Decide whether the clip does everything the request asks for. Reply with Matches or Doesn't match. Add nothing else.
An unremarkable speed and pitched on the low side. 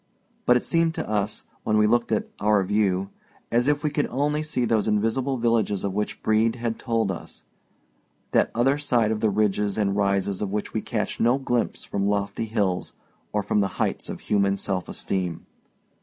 Matches